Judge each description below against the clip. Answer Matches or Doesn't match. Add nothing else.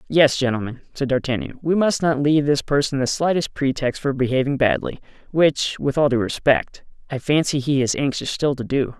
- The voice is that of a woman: Doesn't match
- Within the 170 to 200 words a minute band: Matches